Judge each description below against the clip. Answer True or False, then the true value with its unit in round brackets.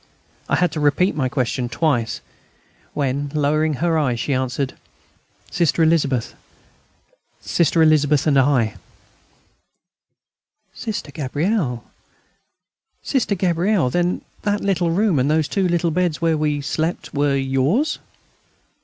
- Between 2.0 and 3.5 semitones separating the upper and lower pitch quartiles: False (3.9 semitones)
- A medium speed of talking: False (120 wpm)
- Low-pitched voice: False (155 Hz)